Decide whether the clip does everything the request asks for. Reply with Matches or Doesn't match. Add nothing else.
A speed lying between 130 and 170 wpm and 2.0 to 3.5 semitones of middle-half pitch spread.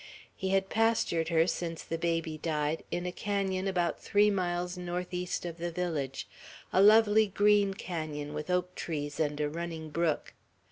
Matches